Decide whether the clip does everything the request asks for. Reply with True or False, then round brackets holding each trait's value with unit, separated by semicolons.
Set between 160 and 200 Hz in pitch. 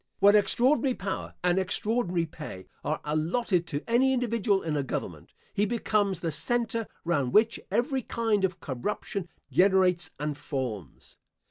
True (190 Hz)